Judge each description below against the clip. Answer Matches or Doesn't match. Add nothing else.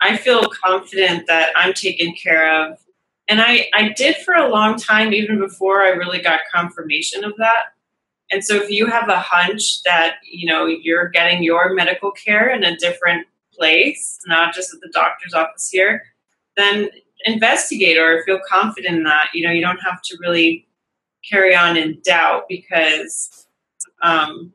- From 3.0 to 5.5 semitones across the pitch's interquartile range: Matches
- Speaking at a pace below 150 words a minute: Doesn't match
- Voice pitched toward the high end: Doesn't match